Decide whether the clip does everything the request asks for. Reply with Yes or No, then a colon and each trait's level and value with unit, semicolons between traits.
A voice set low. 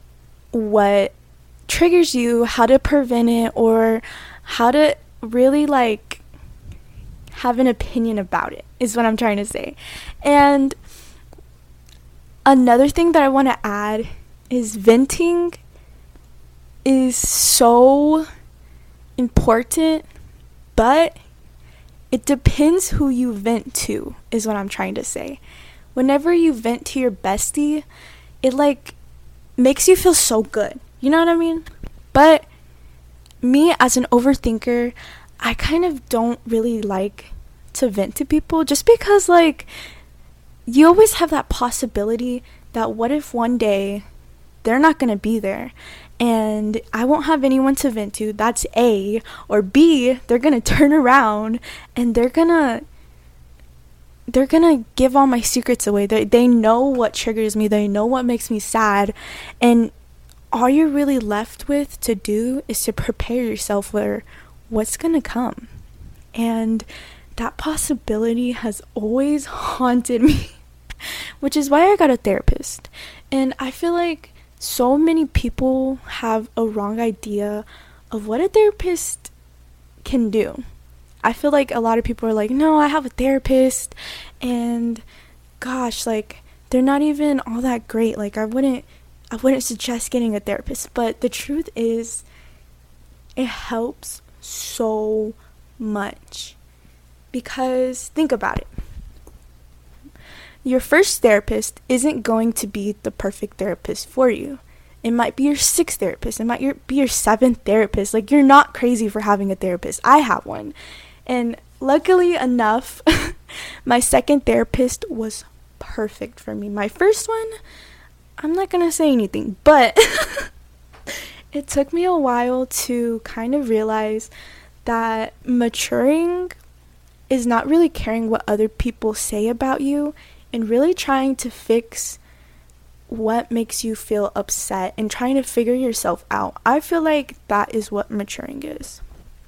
No: high, 235 Hz